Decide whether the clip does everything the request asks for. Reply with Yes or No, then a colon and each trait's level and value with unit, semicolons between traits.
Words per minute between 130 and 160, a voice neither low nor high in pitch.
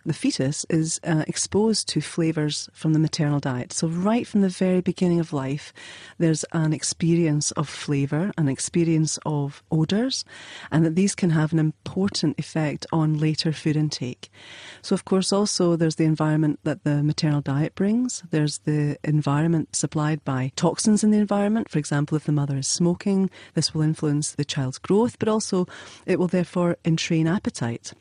No: average, 175 wpm; medium, 160 Hz